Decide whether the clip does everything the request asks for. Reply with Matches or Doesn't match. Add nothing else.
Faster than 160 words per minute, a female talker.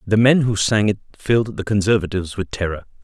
Doesn't match